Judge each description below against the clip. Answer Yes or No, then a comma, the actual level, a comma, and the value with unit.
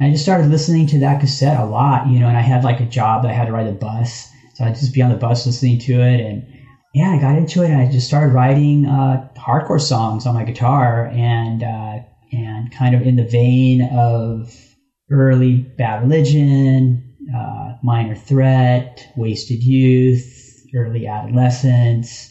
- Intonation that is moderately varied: No, narrow, 2.1 semitones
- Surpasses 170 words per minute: Yes, average, 190 wpm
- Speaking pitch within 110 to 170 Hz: Yes, low, 125 Hz